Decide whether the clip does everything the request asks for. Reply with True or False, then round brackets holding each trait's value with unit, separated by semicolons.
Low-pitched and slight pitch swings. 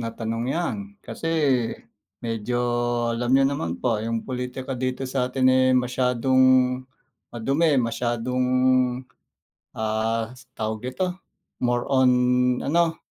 True (125 Hz; 2.3 semitones)